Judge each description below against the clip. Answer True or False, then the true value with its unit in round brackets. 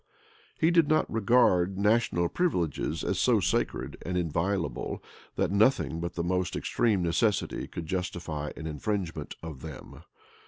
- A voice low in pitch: True (90 Hz)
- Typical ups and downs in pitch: True (4.3 semitones)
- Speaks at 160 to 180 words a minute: False (135 wpm)